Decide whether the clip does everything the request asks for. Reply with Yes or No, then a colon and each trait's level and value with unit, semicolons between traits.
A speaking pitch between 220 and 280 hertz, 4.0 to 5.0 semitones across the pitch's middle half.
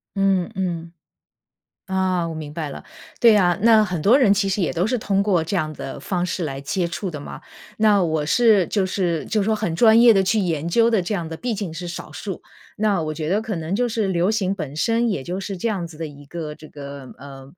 No: medium, 185 Hz; average, 4.5 semitones